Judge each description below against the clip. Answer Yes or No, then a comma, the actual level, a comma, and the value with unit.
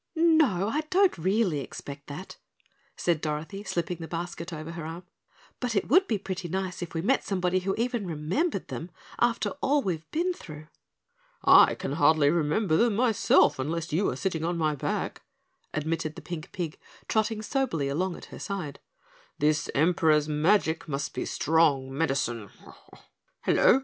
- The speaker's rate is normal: Yes, average, 160 wpm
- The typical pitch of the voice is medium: Yes, medium, 170 Hz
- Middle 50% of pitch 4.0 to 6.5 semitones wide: Yes, average, 4.9 semitones